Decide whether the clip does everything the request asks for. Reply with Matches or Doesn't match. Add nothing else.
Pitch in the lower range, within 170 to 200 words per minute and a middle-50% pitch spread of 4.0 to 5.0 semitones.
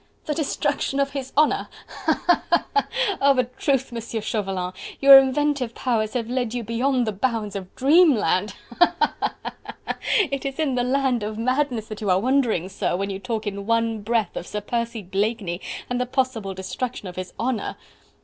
Doesn't match